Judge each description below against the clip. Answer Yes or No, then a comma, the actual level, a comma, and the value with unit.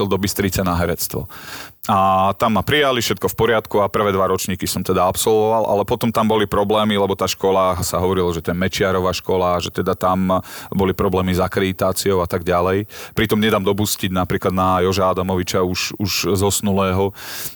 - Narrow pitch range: Yes, narrow, 1.6 semitones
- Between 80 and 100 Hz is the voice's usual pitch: Yes, very low, 95 Hz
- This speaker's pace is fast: Yes, fast, 185 wpm